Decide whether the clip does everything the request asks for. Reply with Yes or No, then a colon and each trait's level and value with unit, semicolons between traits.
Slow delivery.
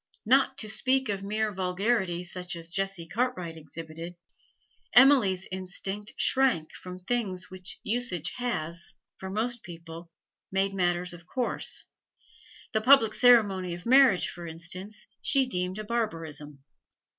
Yes: slow, 130 wpm